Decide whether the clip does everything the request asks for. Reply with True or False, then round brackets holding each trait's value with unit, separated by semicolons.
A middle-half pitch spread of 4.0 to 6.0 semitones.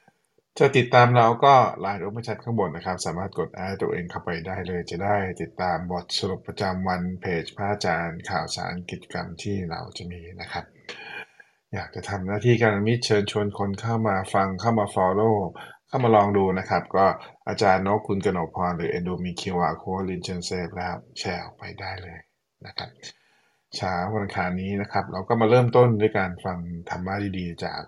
False (2.9 semitones)